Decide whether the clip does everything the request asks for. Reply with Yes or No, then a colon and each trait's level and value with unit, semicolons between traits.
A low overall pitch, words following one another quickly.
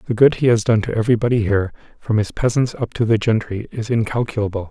Yes: low, 110 Hz; fast, 215 wpm